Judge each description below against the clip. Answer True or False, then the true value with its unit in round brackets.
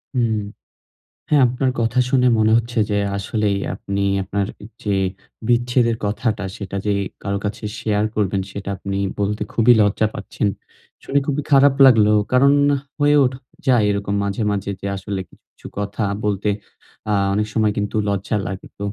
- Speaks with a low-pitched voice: True (105 Hz)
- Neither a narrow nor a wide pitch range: True (3.1 semitones)